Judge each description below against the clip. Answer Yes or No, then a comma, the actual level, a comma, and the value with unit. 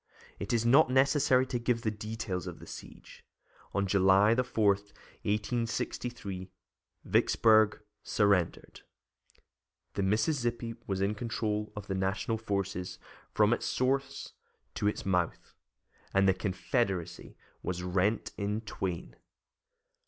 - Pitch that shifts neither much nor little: Yes, average, 3.3 semitones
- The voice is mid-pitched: No, low, 105 Hz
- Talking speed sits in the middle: No, slow, 115 wpm